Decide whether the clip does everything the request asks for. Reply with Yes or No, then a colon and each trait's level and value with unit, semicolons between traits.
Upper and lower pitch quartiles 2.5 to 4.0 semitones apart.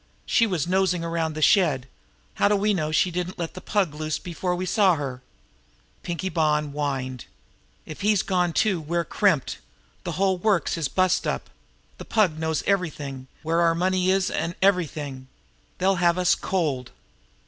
Yes: average, 3.5 semitones